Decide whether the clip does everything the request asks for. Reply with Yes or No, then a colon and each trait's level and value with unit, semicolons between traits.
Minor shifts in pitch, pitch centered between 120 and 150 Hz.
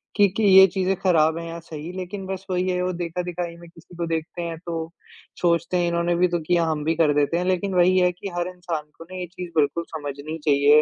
No: narrow, 1.8 semitones; medium, 170 Hz